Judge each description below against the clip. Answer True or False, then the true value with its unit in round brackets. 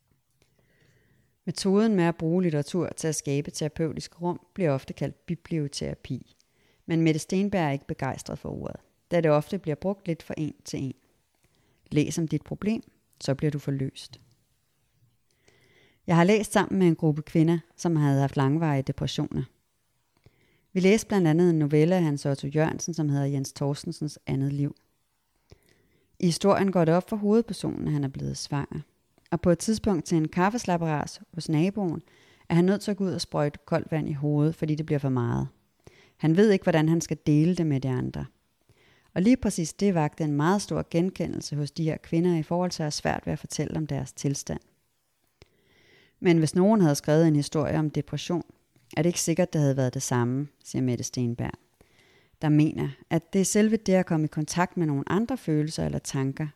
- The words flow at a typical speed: True (195 wpm)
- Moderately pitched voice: True (155 Hz)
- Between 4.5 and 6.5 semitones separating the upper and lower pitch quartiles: False (3.9 semitones)